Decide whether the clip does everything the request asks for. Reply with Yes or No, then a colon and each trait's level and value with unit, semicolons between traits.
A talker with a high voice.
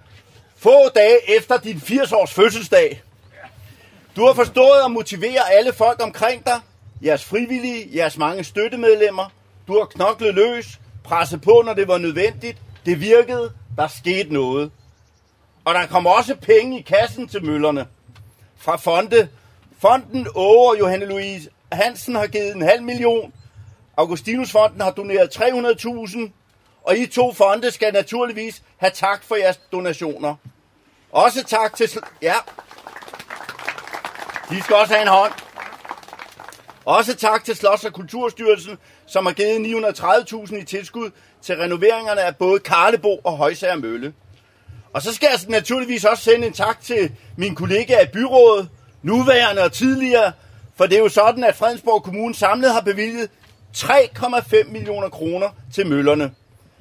Yes: high, 205 Hz